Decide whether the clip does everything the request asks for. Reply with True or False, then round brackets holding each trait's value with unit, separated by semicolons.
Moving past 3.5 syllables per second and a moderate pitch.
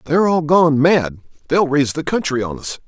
True (5.5 syllables/s; 150 Hz)